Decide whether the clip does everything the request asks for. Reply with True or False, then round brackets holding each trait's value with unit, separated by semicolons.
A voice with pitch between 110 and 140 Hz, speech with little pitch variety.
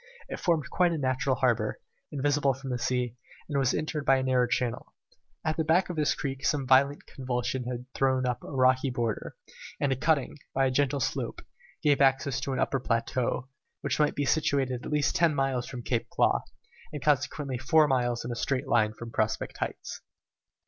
True (135 Hz; 2.3 semitones)